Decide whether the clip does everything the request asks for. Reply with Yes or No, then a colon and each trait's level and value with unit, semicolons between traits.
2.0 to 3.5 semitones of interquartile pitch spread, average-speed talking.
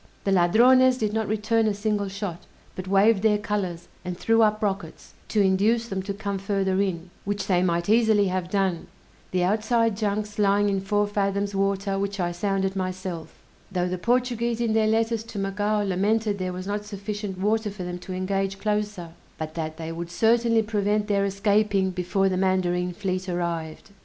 Yes: narrow, 2.4 semitones; average, 180 wpm